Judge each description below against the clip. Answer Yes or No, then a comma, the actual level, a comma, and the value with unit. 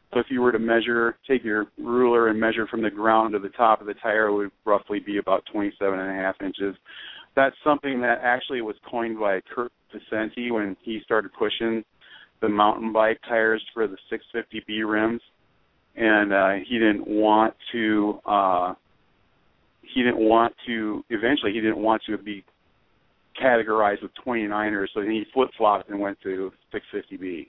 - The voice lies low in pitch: Yes, low, 110 Hz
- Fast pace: No, average, 170 wpm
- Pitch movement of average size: No, narrow, 1.8 semitones